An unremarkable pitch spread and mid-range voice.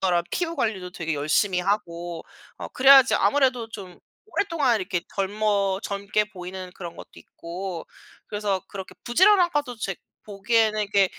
No: average, 4.4 semitones; high, 200 Hz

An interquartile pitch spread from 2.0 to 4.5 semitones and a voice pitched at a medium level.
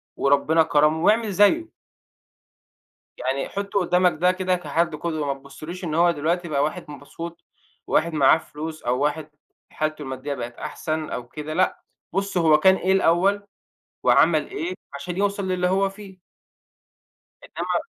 Yes: average, 3.8 semitones; medium, 165 Hz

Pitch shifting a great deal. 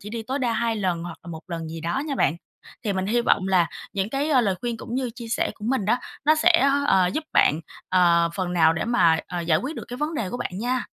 Yes: wide, 6.1 semitones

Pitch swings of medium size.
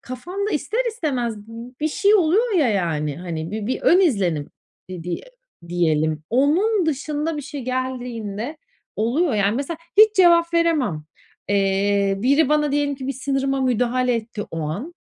No: wide, 7.6 semitones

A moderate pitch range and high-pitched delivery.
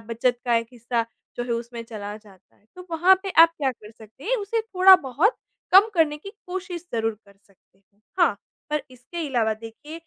No: wide, 7.9 semitones; very high, 255 Hz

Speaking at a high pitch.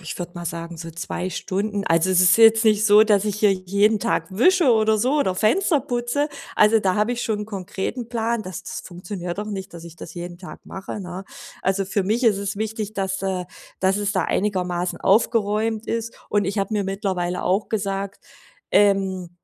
Yes: high, 200 Hz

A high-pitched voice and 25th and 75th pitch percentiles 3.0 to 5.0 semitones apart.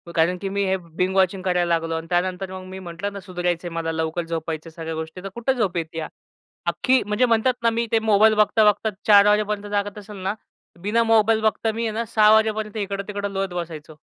Yes: high, 195 Hz; average, 3.6 semitones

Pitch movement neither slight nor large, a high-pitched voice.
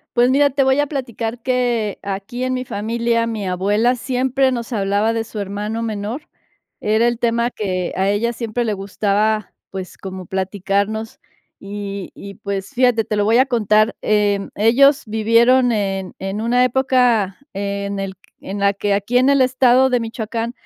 Yes: average, 3.4 semitones; high, 220 Hz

